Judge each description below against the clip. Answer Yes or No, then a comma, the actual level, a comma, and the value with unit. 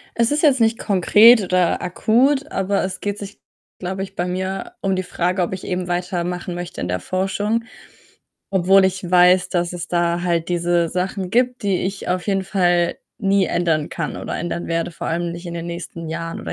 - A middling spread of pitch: No, narrow, 2.2 semitones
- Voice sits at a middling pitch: Yes, medium, 180 Hz